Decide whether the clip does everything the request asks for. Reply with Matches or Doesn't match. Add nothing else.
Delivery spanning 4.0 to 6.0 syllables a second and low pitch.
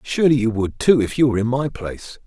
Doesn't match